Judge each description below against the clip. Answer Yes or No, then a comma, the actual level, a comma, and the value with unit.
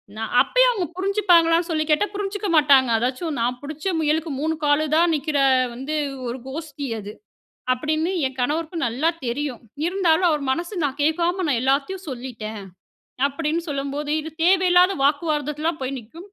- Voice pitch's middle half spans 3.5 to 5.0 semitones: Yes, average, 3.8 semitones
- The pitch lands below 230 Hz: No, very high, 310 Hz